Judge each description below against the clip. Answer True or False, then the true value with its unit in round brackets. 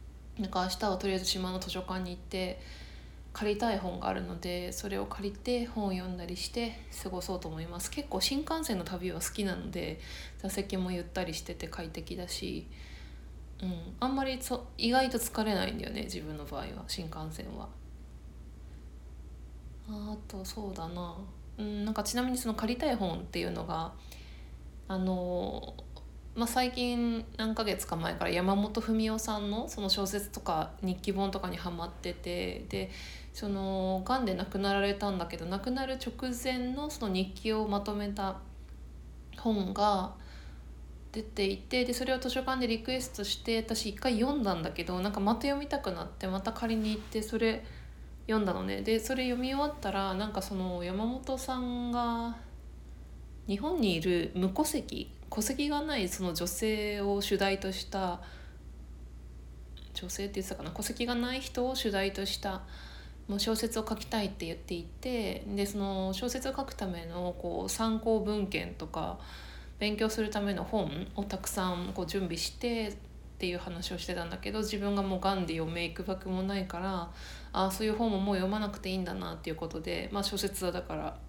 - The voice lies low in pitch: False (195 Hz)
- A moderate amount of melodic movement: True (4.5 semitones)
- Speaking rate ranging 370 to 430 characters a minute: False (330 characters per minute)